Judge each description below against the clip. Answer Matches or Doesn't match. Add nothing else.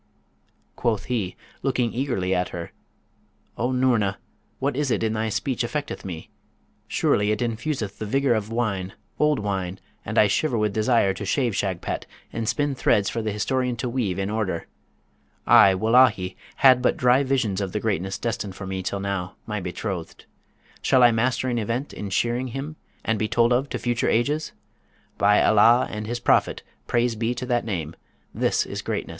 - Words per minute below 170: Doesn't match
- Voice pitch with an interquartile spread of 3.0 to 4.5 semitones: Matches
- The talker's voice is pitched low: Matches